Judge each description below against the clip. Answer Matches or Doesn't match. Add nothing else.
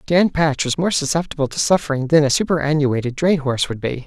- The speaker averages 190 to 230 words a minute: Matches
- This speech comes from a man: Matches